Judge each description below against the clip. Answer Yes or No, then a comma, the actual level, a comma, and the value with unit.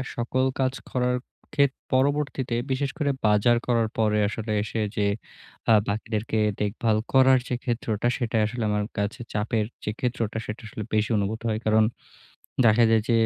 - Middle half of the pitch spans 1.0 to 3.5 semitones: Yes, average, 2.8 semitones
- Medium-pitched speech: No, low, 115 Hz